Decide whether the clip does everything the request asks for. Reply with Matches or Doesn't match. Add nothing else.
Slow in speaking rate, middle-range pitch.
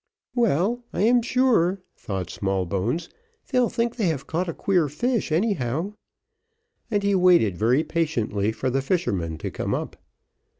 Doesn't match